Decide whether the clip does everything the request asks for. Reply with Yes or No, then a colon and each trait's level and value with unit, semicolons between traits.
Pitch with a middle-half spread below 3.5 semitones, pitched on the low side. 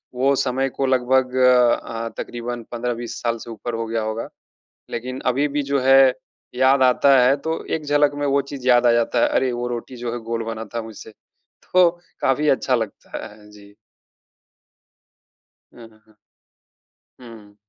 Yes: narrow, 2.5 semitones; low, 125 Hz